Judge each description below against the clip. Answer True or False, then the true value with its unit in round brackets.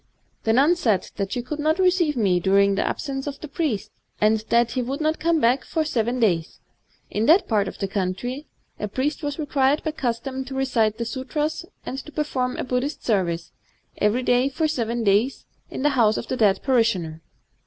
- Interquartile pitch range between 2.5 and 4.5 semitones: False (5.3 semitones)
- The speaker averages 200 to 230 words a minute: True (205 wpm)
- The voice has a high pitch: True (250 Hz)